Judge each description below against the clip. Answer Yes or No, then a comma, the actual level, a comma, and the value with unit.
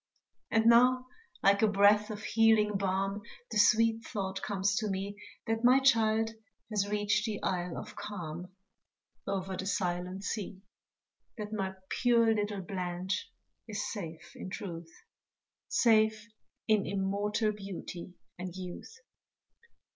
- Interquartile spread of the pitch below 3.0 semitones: Yes, narrow, 2.4 semitones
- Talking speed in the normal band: No, slow, 125 wpm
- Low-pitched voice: No, high, 205 Hz